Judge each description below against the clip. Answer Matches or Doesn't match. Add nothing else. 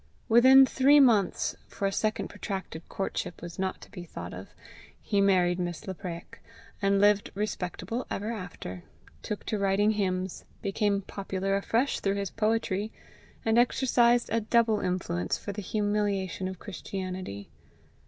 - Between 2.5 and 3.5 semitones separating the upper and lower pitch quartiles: Matches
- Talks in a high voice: Matches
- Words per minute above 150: Doesn't match